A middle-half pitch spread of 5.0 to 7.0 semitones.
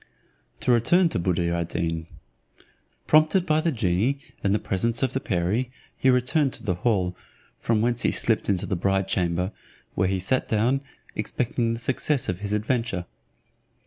Yes: wide, 5.5 semitones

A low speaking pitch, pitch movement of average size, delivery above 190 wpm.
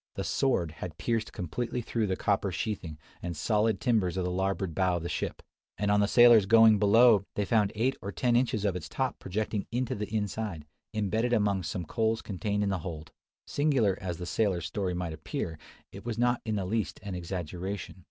Yes: low, 100 Hz; average, 3.6 semitones; average, 200 wpm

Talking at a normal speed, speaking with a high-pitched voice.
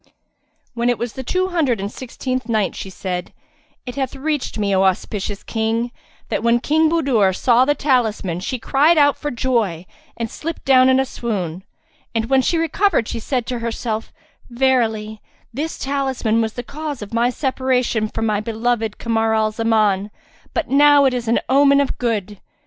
Yes: average, 175 wpm; high, 240 Hz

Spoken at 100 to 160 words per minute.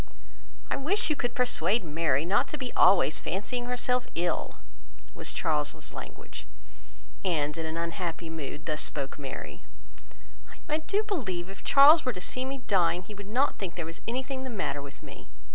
No: average, 175 wpm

